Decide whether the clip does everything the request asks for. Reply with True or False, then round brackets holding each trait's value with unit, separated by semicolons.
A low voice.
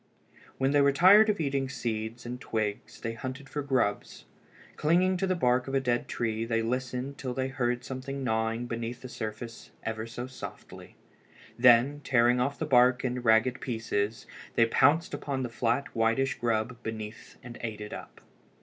True (125 Hz)